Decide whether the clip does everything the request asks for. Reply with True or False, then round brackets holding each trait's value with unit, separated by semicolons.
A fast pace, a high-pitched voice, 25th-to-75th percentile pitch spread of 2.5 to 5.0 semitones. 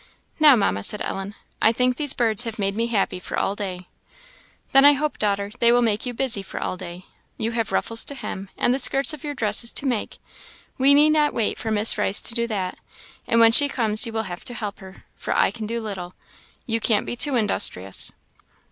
True (225 wpm; 225 Hz; 3.7 semitones)